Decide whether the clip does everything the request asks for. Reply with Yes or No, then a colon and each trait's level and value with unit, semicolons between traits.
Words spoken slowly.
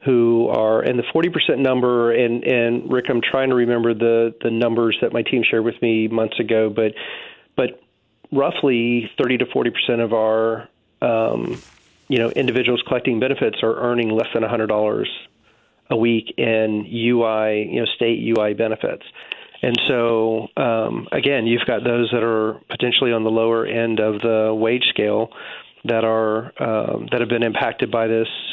No: average, 170 wpm